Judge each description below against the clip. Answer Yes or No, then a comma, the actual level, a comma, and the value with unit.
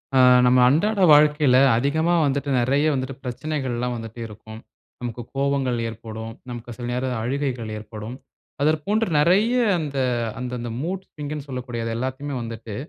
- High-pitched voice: No, low, 130 Hz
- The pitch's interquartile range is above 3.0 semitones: Yes, average, 3.8 semitones